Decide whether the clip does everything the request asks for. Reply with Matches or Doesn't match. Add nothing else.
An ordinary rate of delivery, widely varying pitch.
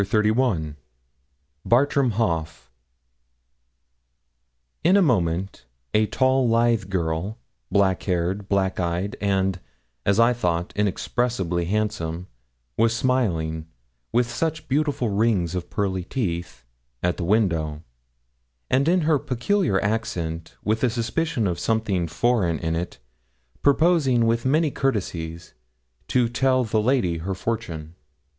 Doesn't match